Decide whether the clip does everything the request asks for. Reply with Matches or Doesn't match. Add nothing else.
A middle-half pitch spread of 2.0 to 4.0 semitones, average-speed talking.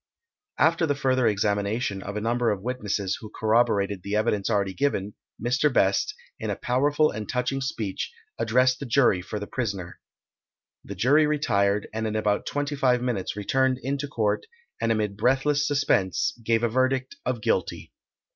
Doesn't match